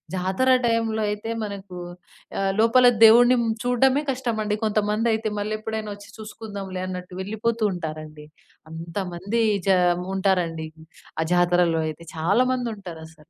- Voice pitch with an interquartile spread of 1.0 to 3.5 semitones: No, average, 4.1 semitones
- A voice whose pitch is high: Yes, high, 205 Hz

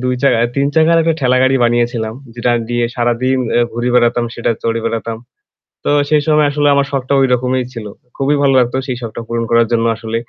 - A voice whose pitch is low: Yes, low, 125 Hz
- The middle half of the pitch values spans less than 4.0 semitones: Yes, narrow, 2.6 semitones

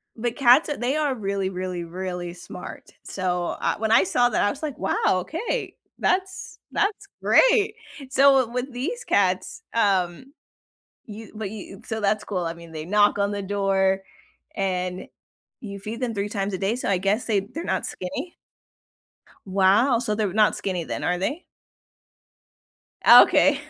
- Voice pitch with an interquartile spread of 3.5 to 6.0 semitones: Yes, average, 4.7 semitones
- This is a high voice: Yes, high, 205 Hz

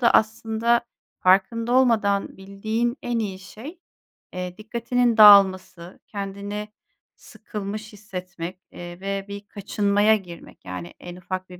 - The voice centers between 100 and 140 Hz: No, high, 200 Hz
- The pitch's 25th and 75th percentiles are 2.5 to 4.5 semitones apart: Yes, average, 2.9 semitones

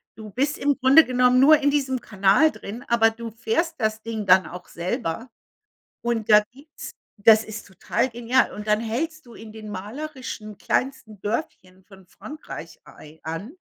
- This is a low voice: No, high, 230 Hz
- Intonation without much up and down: No, average, 3.8 semitones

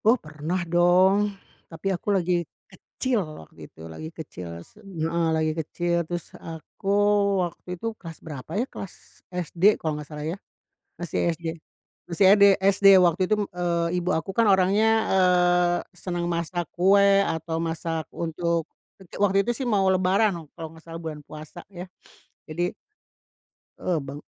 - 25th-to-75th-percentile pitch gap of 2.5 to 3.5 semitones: Yes, average, 2.9 semitones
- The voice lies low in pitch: No, medium, 175 Hz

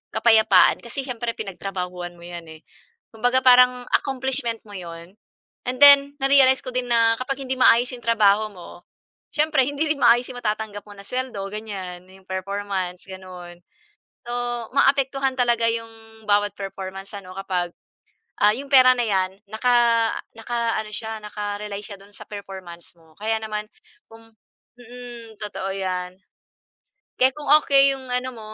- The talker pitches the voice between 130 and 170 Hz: No, high, 220 Hz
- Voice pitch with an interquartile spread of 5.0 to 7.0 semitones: No, average, 4.4 semitones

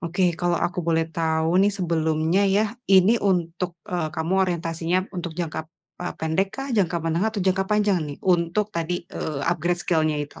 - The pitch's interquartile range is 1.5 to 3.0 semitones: Yes, narrow, 2.6 semitones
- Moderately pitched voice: Yes, medium, 175 Hz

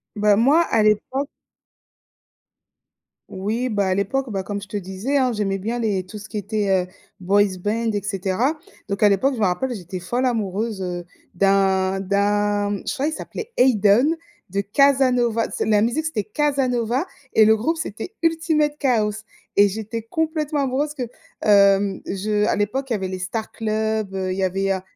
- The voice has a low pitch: No, high, 215 Hz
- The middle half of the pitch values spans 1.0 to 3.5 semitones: No, average, 4.4 semitones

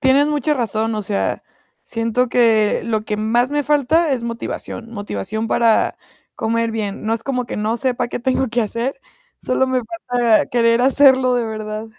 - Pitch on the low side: No, high, 235 Hz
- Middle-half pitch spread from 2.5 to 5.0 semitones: Yes, average, 2.8 semitones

